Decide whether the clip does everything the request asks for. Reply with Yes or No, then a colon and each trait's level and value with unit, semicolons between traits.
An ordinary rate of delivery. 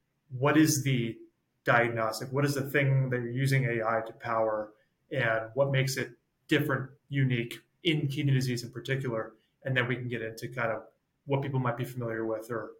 Yes: average, 190 wpm